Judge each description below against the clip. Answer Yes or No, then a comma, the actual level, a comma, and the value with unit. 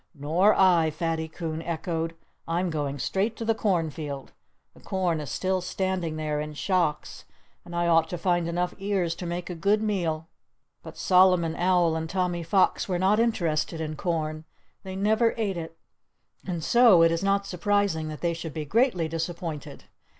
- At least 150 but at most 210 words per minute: Yes, average, 170 wpm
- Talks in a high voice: No, medium, 170 Hz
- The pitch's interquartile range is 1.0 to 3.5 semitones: Yes, average, 2.9 semitones